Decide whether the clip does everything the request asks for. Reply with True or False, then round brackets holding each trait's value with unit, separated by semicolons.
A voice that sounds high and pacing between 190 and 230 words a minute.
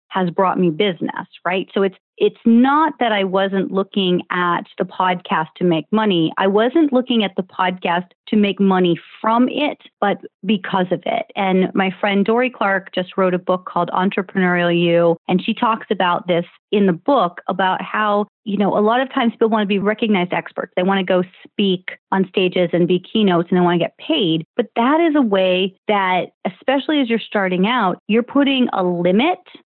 True (195 Hz; 200 wpm)